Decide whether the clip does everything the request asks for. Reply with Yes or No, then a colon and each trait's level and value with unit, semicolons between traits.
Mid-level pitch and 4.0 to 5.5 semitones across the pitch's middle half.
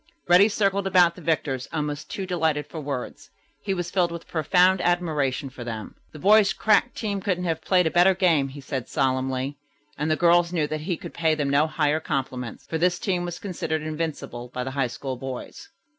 Yes: medium, 160 Hz; average, 4.4 semitones